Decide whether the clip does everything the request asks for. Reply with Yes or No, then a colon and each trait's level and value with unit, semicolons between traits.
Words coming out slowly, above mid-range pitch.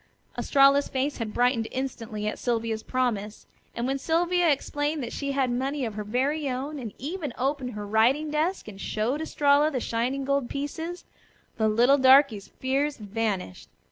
No: average, 165 wpm; very high, 260 Hz